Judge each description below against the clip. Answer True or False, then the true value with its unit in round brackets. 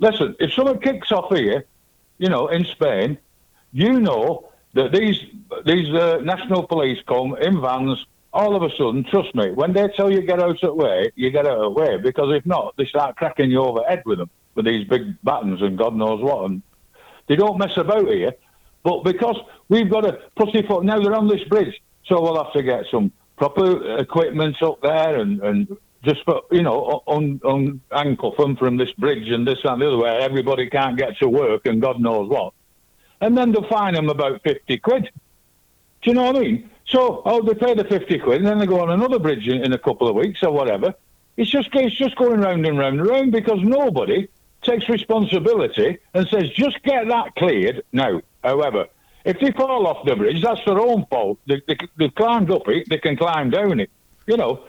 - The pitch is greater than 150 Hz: True (185 Hz)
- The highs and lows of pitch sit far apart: True (7.9 semitones)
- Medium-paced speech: False (215 wpm)